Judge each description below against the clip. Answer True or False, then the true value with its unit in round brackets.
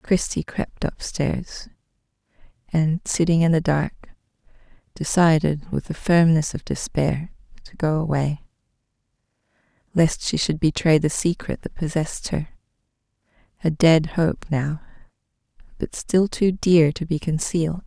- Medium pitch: True (160 Hz)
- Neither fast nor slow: False (125 wpm)